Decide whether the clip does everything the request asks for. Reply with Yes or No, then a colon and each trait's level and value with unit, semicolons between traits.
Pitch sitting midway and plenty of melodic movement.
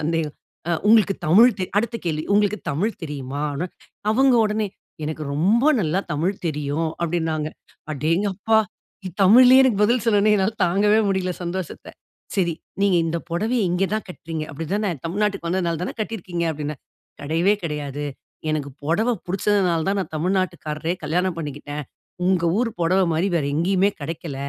No: medium, 175 Hz; average, 4.6 semitones